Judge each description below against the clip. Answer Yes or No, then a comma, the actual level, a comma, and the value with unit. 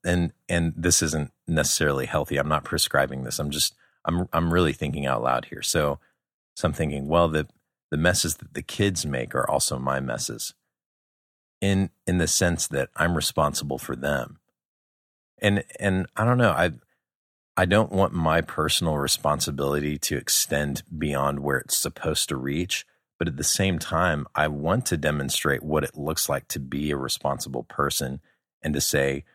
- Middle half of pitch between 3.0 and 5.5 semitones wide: Yes, average, 3.9 semitones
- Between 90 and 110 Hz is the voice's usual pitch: No, very low, 75 Hz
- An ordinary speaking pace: Yes, average, 175 wpm